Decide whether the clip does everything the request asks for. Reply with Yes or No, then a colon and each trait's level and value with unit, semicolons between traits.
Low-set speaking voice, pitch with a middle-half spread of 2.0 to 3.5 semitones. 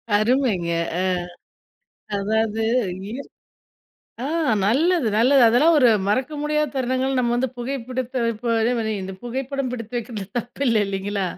No: high, 240 Hz; average, 3.2 semitones